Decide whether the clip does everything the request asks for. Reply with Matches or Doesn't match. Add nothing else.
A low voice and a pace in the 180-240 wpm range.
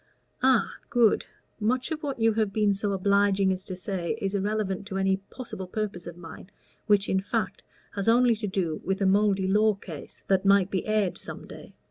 Doesn't match